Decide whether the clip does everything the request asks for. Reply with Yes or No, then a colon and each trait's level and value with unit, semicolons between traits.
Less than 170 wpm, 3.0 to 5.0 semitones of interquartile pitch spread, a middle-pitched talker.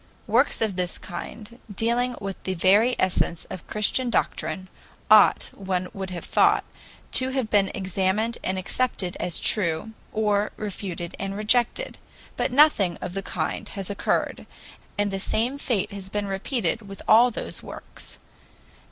No: average, 150 wpm; average, 3.3 semitones; high, 200 Hz